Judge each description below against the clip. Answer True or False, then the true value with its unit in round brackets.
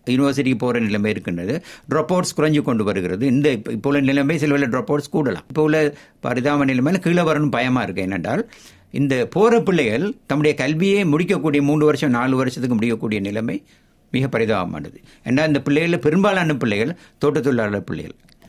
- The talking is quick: True (155 wpm)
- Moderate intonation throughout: True (3.9 semitones)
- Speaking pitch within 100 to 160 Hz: True (140 Hz)